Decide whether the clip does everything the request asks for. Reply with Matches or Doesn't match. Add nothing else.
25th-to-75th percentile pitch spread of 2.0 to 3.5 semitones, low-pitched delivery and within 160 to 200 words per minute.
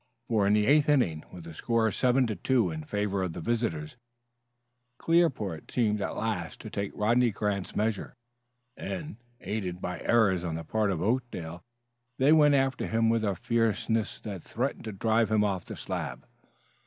Doesn't match